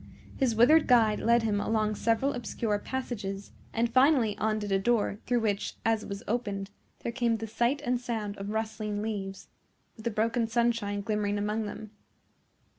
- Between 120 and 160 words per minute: No, average, 170 wpm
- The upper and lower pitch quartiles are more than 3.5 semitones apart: No, narrow, 2.4 semitones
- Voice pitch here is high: Yes, high, 220 Hz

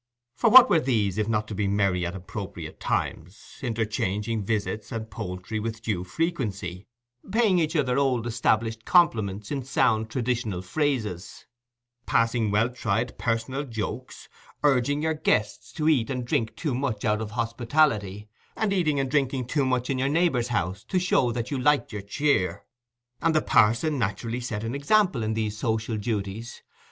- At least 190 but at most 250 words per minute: No, average, 165 wpm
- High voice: No, low, 115 Hz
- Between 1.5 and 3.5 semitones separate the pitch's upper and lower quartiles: No, average, 4.6 semitones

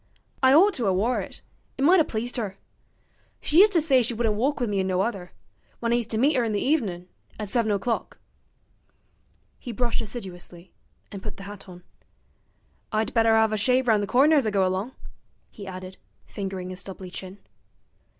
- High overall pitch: Yes, high, 220 Hz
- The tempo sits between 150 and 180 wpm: No, average, 200 wpm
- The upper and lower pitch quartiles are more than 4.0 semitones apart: Yes, average, 4.4 semitones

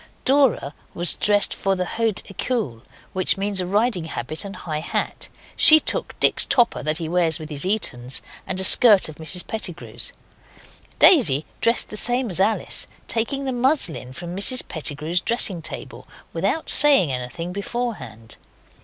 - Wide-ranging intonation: Yes, wide, 6.5 semitones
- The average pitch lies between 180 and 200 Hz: Yes, high, 190 Hz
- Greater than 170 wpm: No, average, 160 wpm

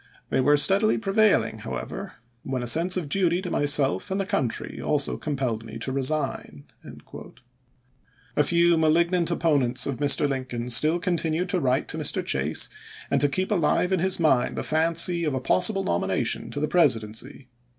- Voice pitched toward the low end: No, medium, 150 Hz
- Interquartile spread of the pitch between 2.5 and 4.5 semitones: No, average, 5.0 semitones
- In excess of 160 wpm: Yes, average, 170 wpm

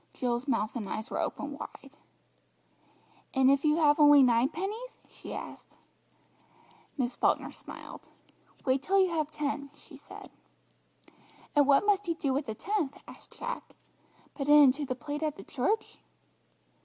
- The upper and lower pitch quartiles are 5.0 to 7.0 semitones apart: No, average, 3.3 semitones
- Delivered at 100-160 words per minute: Yes, average, 155 wpm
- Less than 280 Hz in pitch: No, very high, 285 Hz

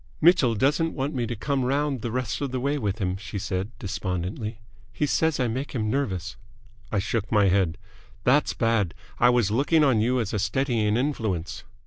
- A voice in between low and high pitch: No, low, 115 Hz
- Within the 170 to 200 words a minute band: Yes, average, 190 wpm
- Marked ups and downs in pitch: No, average, 4.9 semitones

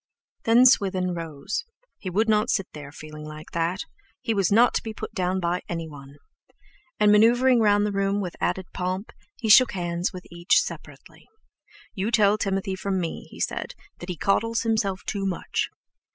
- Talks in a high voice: Yes, high, 195 Hz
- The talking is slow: No, average, 170 wpm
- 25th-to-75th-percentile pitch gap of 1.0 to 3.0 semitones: No, average, 3.8 semitones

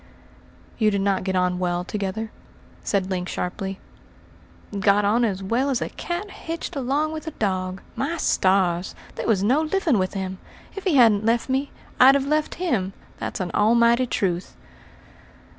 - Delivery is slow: No, average, 165 wpm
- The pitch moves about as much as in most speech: No, wide, 6.3 semitones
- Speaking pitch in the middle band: No, high, 215 Hz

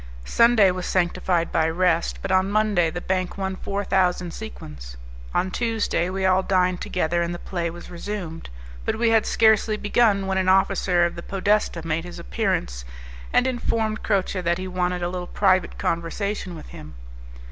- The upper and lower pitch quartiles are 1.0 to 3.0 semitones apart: Yes, narrow, 2.6 semitones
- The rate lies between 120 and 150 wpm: No, average, 180 wpm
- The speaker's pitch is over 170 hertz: Yes, medium, 185 Hz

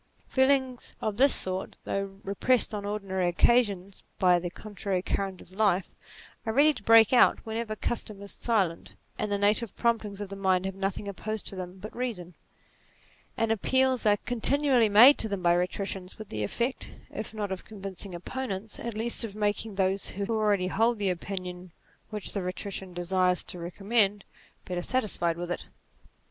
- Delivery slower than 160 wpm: No, average, 175 wpm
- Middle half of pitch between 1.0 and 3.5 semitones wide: Yes, average, 3.2 semitones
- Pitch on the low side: No, high, 200 Hz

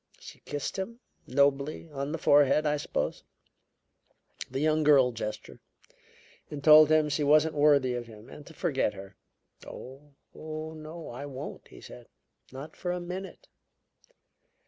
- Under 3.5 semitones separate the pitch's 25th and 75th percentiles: Yes, narrow, 2.4 semitones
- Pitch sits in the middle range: Yes, medium, 150 Hz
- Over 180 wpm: No, average, 145 wpm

